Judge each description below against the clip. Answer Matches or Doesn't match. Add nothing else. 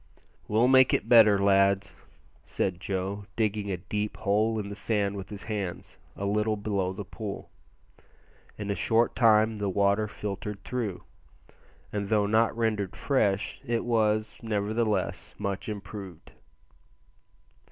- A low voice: Matches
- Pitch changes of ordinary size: Doesn't match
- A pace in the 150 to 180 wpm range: Doesn't match